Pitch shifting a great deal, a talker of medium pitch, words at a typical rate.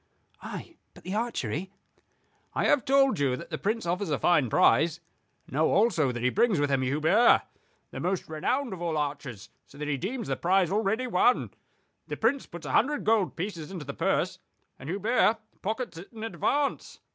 Yes: wide, 7.2 semitones; medium, 180 Hz; average, 185 wpm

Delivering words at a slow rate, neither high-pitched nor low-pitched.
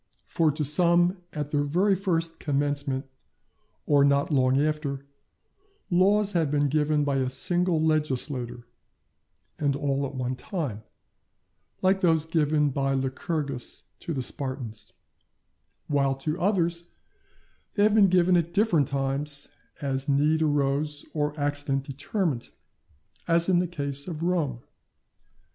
Yes: slow, 130 wpm; medium, 150 Hz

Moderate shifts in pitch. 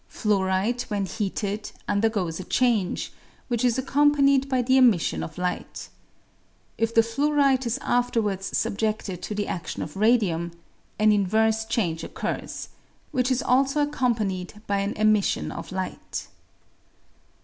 Yes: average, 4.3 semitones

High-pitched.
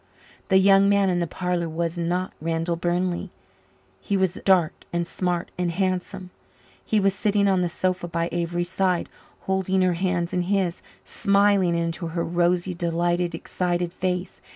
No: medium, 180 Hz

